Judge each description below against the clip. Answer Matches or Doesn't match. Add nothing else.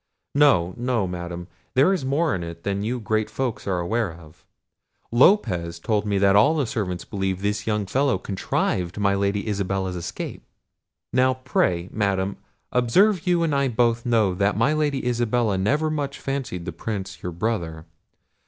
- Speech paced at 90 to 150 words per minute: Doesn't match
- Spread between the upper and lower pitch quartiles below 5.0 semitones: Doesn't match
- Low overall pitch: Matches